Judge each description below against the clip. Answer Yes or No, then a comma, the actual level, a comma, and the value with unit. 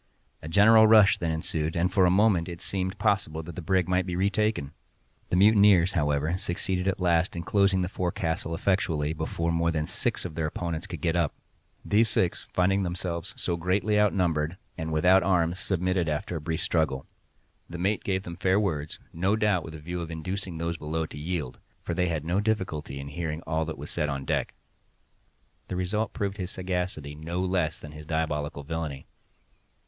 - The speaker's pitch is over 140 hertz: No, very low, 85 Hz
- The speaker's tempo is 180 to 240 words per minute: Yes, average, 190 wpm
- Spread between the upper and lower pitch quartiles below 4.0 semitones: Yes, average, 2.9 semitones